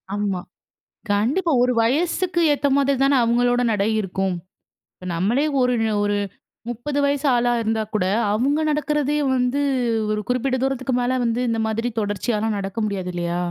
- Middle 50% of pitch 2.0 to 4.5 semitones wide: No, average, 5.0 semitones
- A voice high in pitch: Yes, high, 240 Hz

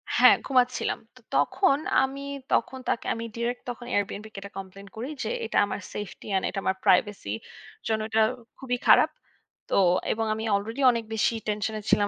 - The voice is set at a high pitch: Yes, high, 220 Hz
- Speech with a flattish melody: No, average, 3.3 semitones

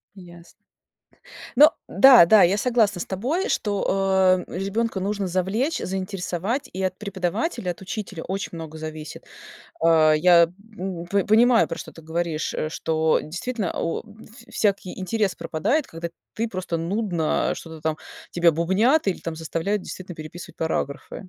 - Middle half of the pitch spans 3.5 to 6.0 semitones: Yes, average, 3.9 semitones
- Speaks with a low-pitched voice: No, medium, 185 Hz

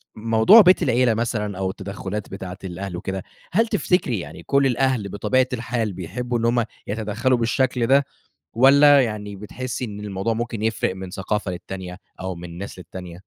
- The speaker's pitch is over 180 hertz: No, low, 110 Hz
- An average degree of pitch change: Yes, average, 4.6 semitones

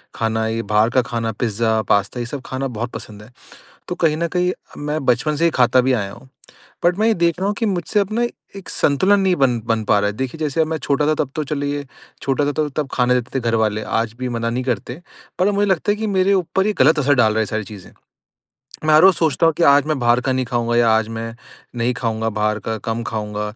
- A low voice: Yes, low, 130 Hz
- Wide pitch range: Yes, wide, 5.7 semitones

